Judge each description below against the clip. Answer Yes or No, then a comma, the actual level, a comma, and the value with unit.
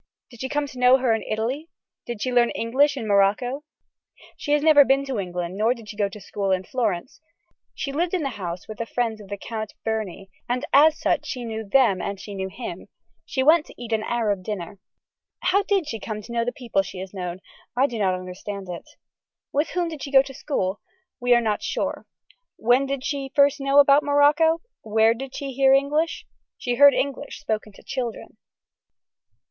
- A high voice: Yes, high, 240 Hz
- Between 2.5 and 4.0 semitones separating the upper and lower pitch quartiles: No, average, 5.1 semitones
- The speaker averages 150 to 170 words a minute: No, fast, 205 wpm